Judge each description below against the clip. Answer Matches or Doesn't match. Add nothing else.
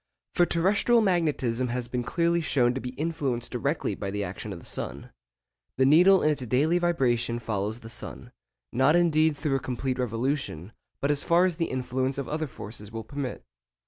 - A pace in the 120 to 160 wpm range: Doesn't match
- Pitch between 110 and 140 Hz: Matches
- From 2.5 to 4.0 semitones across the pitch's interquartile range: Doesn't match